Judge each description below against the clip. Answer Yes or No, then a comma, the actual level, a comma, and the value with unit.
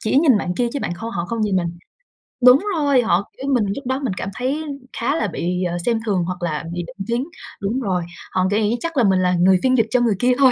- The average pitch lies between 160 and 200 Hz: No, high, 220 Hz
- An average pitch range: No, wide, 5.8 semitones